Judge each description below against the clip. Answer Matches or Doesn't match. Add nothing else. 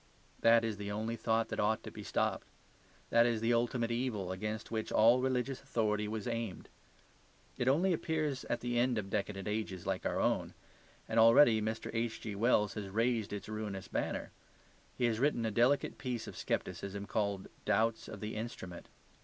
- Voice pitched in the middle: Doesn't match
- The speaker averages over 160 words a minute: Matches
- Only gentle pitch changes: Matches